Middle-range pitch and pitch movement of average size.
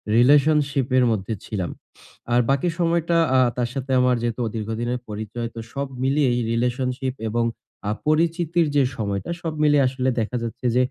No: low, 130 Hz; average, 3.6 semitones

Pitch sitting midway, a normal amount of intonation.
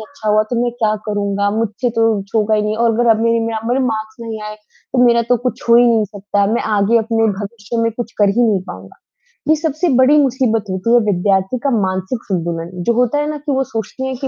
No: high, 225 Hz; average, 3.0 semitones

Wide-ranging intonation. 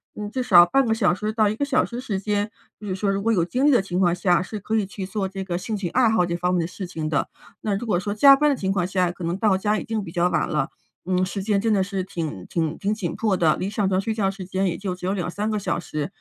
No: average, 3.1 semitones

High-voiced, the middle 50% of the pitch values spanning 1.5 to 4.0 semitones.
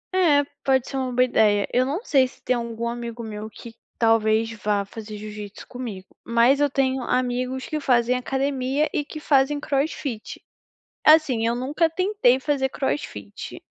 Yes: very high, 250 Hz; average, 3.5 semitones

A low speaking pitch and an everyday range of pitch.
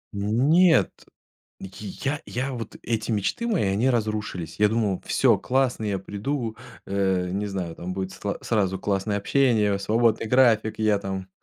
Yes: low, 105 Hz; average, 3.5 semitones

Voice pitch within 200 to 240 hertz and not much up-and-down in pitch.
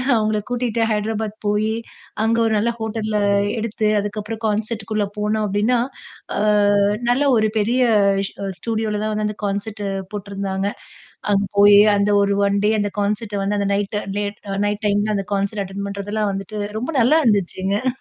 Yes: high, 210 Hz; narrow, 1.4 semitones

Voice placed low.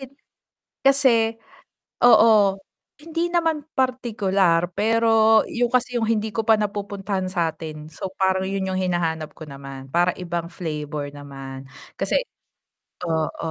No: high, 190 Hz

